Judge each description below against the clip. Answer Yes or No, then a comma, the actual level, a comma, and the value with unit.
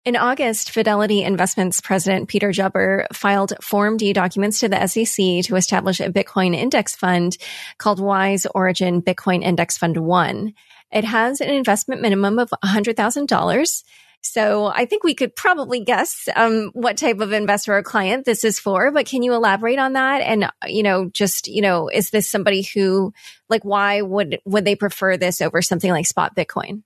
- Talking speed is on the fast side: No, average, 175 wpm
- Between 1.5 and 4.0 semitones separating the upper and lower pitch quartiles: Yes, average, 2.8 semitones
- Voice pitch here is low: No, high, 205 Hz